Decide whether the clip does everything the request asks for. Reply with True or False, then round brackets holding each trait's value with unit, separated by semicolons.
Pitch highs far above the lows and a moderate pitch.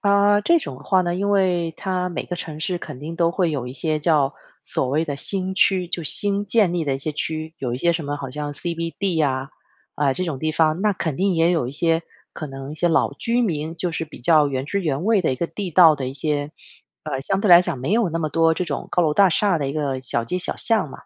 False (4.0 semitones; 165 Hz)